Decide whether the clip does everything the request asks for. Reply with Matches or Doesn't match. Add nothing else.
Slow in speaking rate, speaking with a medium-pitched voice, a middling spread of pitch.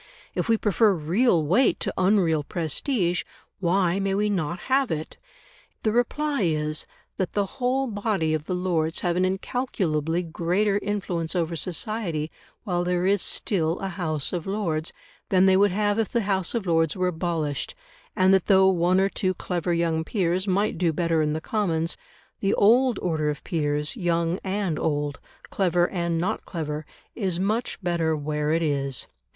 Doesn't match